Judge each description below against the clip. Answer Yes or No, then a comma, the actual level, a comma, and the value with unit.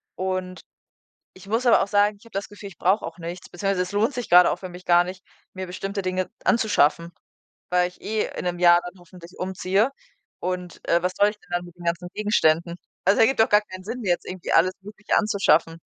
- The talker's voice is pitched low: No, medium, 185 Hz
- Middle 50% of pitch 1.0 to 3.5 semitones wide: Yes, narrow, 2.6 semitones